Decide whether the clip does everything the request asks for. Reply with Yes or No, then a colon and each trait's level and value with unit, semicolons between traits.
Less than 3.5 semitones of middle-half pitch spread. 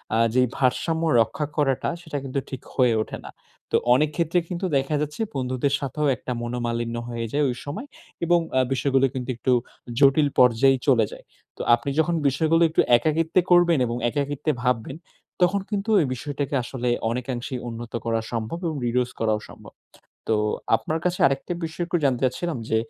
No: average, 4.4 semitones